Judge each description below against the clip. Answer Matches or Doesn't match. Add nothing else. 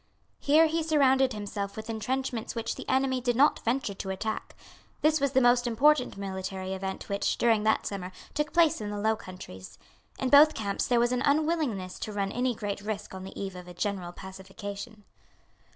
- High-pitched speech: Matches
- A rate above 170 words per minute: Matches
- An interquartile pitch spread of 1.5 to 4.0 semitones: Doesn't match